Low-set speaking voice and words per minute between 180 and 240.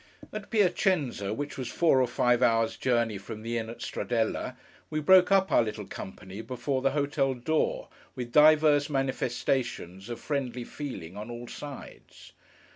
No: low, 125 Hz; average, 155 wpm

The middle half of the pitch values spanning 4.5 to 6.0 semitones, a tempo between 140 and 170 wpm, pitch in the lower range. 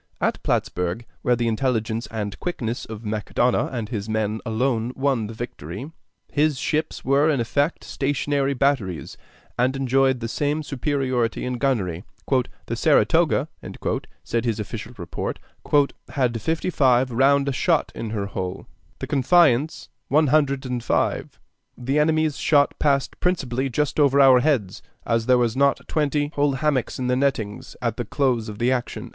No: average, 3.8 semitones; average, 155 wpm; low, 130 Hz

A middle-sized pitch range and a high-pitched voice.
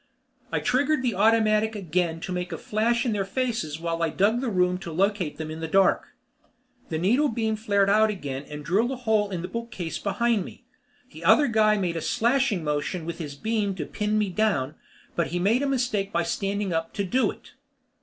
Yes: average, 4.7 semitones; high, 200 Hz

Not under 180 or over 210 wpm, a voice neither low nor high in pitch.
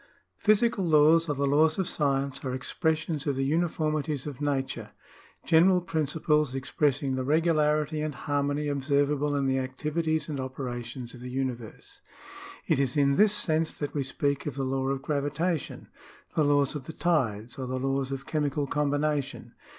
No: average, 165 wpm; medium, 145 Hz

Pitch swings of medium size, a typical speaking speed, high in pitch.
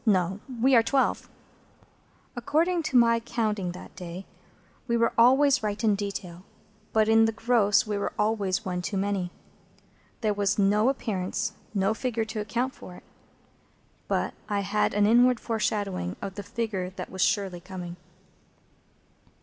Yes: average, 3.3 semitones; average, 150 wpm; high, 210 Hz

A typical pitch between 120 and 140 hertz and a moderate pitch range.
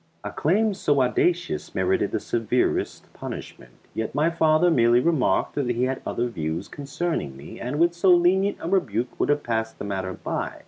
No: low, 135 Hz; wide, 7.3 semitones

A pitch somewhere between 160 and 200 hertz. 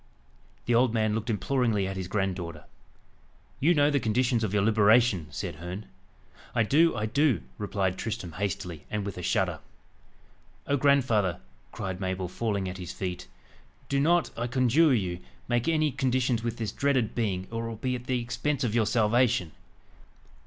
No: low, 110 Hz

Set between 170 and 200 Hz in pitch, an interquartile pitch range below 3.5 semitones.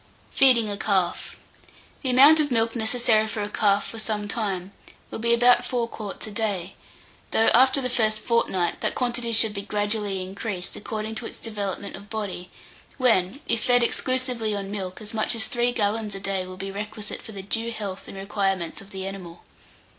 No: high, 215 Hz; average, 2.9 semitones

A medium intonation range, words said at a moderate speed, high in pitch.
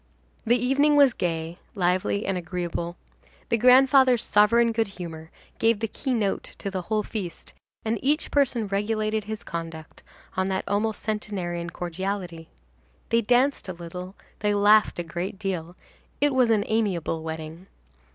Yes: average, 4.6 semitones; average, 150 wpm; high, 205 Hz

